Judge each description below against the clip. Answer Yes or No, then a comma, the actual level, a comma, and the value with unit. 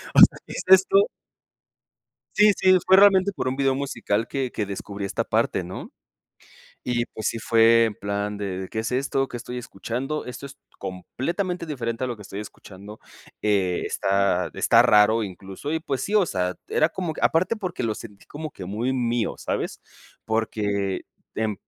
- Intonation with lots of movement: Yes, wide, 5.7 semitones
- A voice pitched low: Yes, low, 115 Hz